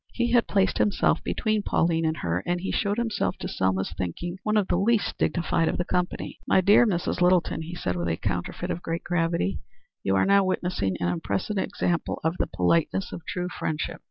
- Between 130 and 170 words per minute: No, fast, 205 wpm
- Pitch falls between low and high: Yes, medium, 175 Hz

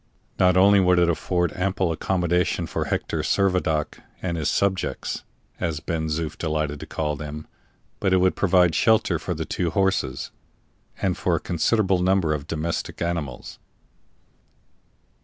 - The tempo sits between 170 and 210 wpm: No, average, 145 wpm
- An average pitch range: Yes, average, 3.0 semitones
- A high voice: No, very low, 85 Hz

